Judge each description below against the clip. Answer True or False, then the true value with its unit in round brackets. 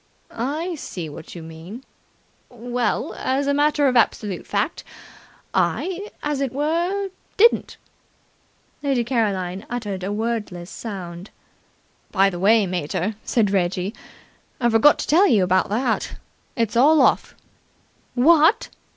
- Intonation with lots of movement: True (6.8 semitones)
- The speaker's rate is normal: False (125 wpm)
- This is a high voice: True (230 Hz)